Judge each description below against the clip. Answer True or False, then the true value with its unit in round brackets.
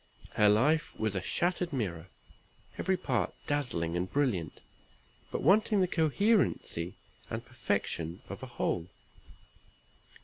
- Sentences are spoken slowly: True (115 wpm)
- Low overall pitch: True (120 Hz)